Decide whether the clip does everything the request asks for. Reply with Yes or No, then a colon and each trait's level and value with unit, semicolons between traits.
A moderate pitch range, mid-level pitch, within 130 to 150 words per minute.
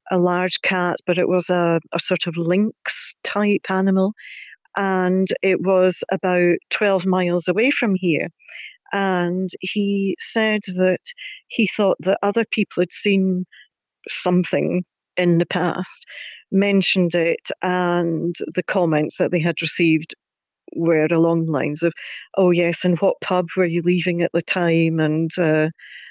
No: narrow, 1.9 semitones; medium, 180 Hz; average, 145 wpm